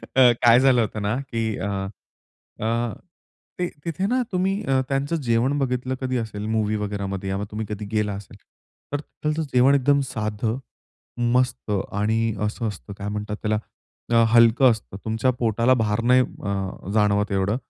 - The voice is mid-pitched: No, low, 115 Hz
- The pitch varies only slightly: No, average, 3.5 semitones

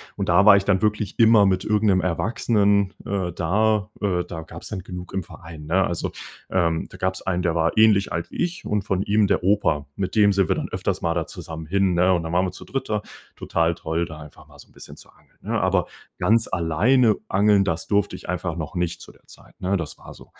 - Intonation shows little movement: No, average, 3.4 semitones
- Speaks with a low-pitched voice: Yes, very low, 95 Hz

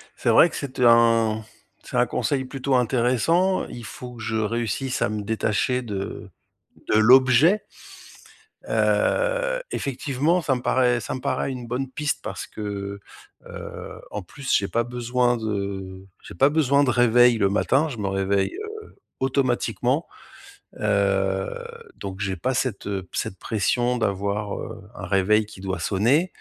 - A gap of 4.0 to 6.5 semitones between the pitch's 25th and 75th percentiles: Yes, average, 4.6 semitones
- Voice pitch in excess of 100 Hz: Yes, low, 120 Hz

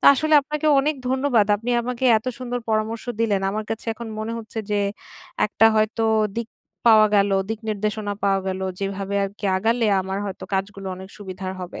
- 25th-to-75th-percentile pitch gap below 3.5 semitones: Yes, average, 2.9 semitones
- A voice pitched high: Yes, high, 215 Hz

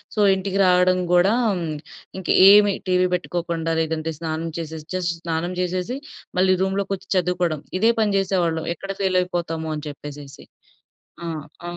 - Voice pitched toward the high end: No, medium, 180 Hz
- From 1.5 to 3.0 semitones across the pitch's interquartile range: Yes, average, 2.7 semitones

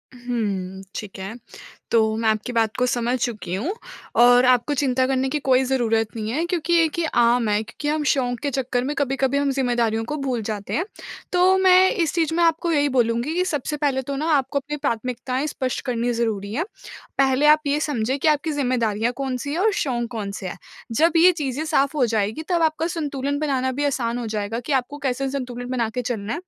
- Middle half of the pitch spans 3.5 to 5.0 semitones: Yes, average, 4.0 semitones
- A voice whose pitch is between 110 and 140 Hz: No, very high, 260 Hz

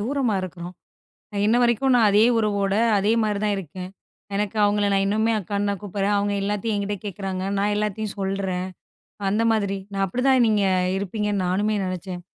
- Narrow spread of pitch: Yes, narrow, 1.5 semitones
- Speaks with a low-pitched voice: No, high, 205 Hz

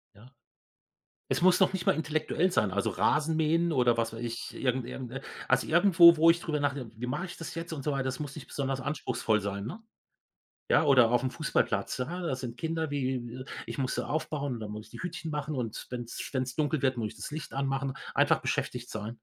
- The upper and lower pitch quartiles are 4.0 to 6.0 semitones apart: Yes, average, 4.3 semitones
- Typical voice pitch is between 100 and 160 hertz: Yes, low, 135 Hz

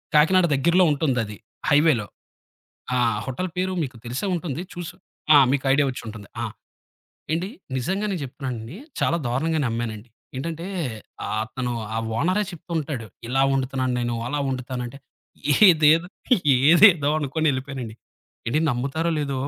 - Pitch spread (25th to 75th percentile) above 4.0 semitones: Yes, average, 4.7 semitones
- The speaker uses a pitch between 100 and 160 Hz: Yes, medium, 140 Hz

